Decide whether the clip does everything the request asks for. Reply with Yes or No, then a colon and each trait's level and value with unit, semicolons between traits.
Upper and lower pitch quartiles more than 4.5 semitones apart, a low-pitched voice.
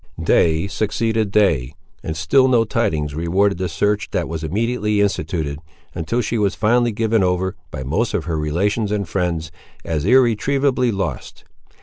Yes: wide, 5.6 semitones; low, 100 Hz